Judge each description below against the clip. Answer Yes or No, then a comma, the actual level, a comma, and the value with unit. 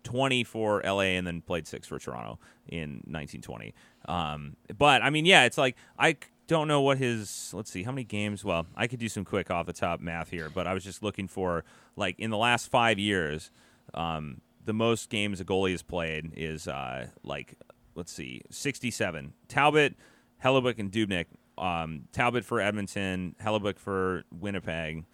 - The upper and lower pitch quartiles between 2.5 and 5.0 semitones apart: No, wide, 5.5 semitones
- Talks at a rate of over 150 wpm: Yes, average, 180 wpm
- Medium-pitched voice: No, low, 100 Hz